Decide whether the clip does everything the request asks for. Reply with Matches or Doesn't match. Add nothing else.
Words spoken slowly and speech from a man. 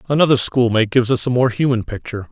Doesn't match